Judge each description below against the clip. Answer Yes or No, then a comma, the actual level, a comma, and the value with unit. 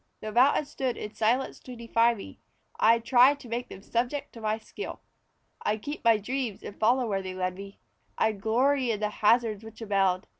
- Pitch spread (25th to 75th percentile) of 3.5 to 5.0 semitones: No, average, 2.9 semitones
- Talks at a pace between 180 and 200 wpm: Yes, average, 195 wpm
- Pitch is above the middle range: Yes, high, 225 Hz